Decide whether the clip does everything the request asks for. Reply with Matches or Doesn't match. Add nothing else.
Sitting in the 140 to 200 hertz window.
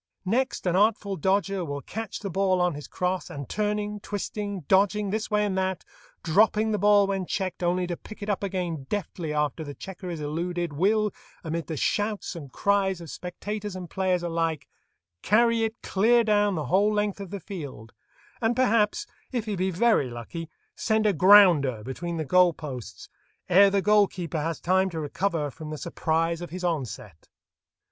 Matches